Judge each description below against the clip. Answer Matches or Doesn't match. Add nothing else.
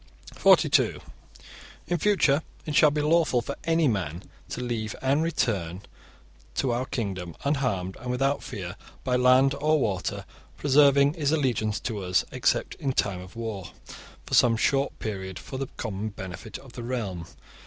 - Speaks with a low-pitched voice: Matches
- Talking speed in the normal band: Matches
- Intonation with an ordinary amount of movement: Doesn't match